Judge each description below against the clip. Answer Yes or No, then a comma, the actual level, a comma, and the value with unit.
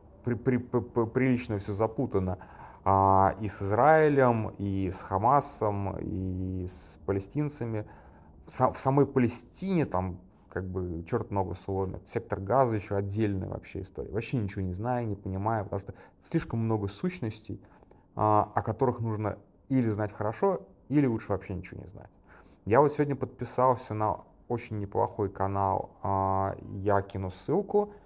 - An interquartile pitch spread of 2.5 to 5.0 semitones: Yes, average, 3.9 semitones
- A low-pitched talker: Yes, low, 105 Hz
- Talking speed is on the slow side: No, average, 145 wpm